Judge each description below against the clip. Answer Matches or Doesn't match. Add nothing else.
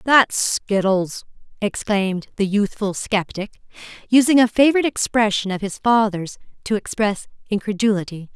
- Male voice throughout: Doesn't match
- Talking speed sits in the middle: Doesn't match